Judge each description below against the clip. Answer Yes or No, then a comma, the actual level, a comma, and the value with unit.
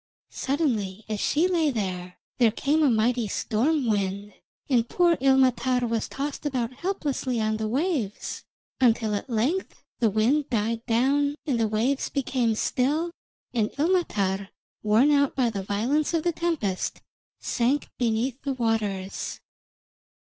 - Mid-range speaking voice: No, high, 245 Hz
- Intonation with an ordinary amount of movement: Yes, average, 4.8 semitones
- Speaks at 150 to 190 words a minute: No, average, 140 wpm